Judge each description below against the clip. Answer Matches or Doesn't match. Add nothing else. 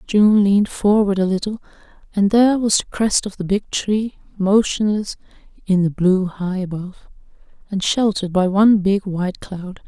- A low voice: Doesn't match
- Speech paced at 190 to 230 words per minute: Doesn't match